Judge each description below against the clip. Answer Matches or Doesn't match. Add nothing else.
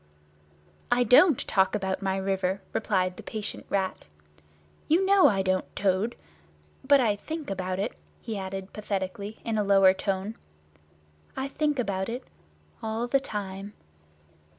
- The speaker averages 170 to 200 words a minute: Doesn't match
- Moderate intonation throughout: Matches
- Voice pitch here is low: Doesn't match